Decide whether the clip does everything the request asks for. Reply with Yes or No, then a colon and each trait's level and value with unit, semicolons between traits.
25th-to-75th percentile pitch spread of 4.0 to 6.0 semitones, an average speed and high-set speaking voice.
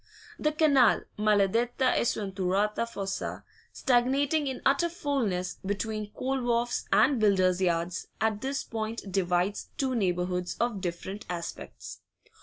No: average, 5.1 semitones; slow, 120 wpm; high, 215 Hz